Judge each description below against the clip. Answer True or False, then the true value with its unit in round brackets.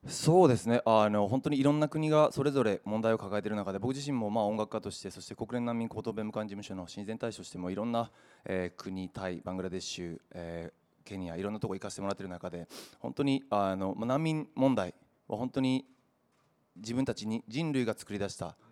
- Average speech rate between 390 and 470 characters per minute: True (425 characters per minute)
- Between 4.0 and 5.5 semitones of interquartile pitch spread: True (5.1 semitones)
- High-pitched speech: False (110 Hz)